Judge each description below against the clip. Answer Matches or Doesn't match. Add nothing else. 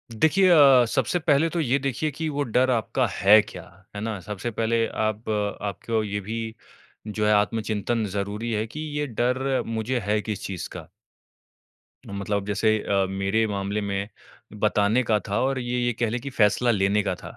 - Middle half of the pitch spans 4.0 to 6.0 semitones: Doesn't match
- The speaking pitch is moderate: Doesn't match